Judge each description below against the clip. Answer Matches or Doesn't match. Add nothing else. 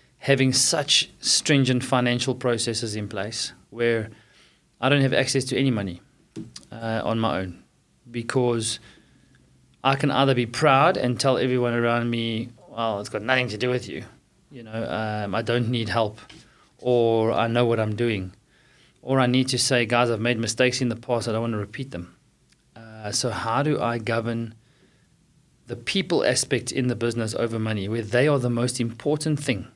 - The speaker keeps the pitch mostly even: Matches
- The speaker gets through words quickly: Doesn't match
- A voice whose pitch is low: Matches